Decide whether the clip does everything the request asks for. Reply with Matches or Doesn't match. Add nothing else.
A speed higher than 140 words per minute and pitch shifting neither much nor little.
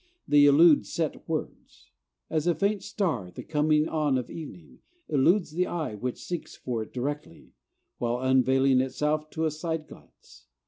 Matches